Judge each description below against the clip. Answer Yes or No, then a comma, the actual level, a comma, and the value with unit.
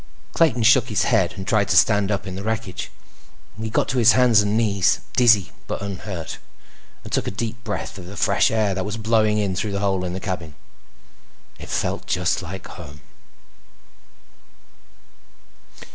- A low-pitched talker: Yes, low, 105 Hz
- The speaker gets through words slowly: No, average, 175 wpm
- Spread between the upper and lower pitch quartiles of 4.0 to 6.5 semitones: No, average, 2.8 semitones